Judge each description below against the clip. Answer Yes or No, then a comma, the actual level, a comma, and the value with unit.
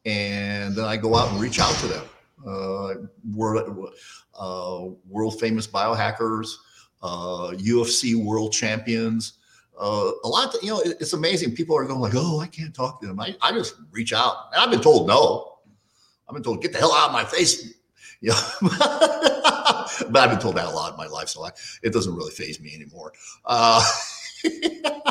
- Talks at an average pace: Yes, average, 195 wpm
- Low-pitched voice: Yes, low, 115 Hz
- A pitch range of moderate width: No, wide, 7.5 semitones